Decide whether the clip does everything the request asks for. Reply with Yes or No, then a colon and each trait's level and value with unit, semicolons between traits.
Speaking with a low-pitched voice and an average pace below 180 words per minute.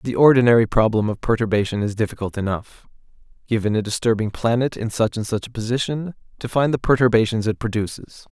Yes: low, 115 Hz; average, 170 wpm